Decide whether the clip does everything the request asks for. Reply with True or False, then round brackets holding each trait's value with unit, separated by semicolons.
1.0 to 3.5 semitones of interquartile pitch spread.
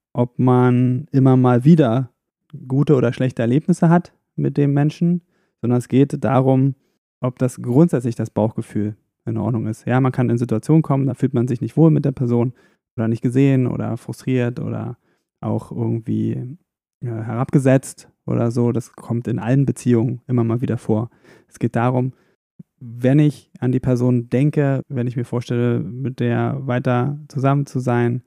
True (2.5 semitones)